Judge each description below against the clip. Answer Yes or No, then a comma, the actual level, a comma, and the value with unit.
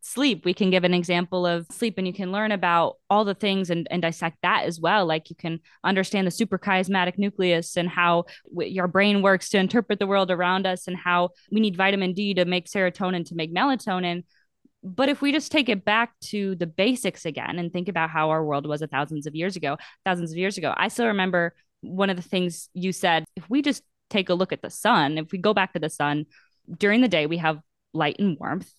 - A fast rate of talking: Yes, fast, 235 wpm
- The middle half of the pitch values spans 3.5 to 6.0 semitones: No, average, 3.0 semitones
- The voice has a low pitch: No, medium, 185 Hz